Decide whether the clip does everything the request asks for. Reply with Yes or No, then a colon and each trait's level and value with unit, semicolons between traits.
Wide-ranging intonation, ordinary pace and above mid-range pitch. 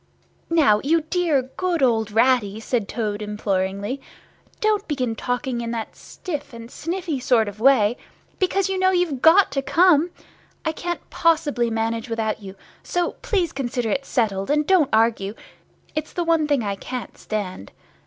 Yes: wide, 6.8 semitones; average, 160 wpm; very high, 255 Hz